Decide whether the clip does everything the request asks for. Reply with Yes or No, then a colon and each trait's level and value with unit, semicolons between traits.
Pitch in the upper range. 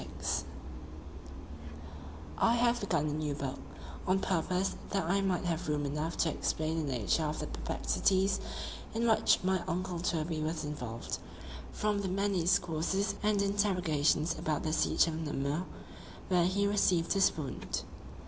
No: medium, 170 Hz